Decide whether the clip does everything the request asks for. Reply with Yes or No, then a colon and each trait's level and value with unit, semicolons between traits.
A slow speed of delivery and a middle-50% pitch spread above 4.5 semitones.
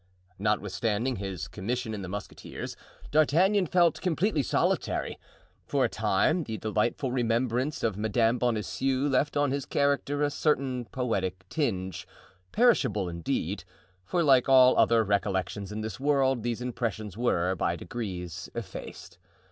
Yes: slow, 130 wpm; wide, 5.4 semitones